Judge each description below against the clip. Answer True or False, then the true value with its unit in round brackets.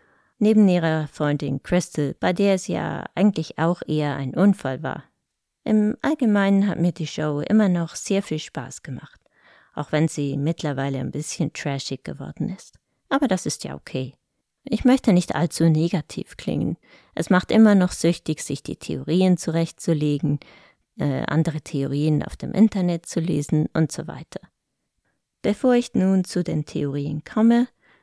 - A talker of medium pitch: True (165 Hz)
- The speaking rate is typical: True (155 wpm)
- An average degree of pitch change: True (4.8 semitones)